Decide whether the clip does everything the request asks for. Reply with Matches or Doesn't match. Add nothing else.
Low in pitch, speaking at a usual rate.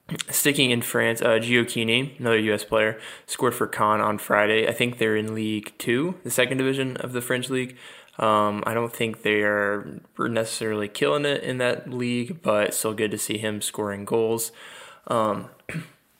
Matches